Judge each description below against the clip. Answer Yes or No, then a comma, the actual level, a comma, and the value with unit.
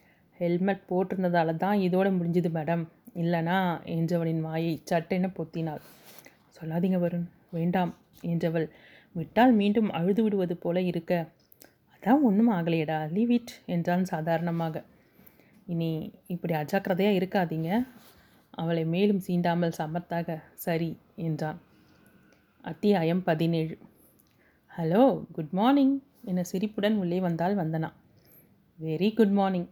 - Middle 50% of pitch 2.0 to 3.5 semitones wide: Yes, average, 2.9 semitones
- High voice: No, medium, 175 Hz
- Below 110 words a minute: Yes, average, 100 wpm